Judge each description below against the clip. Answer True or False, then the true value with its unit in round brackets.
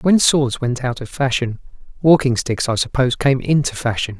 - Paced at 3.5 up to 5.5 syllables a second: True (5.1 syllables/s)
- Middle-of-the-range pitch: False (130 Hz)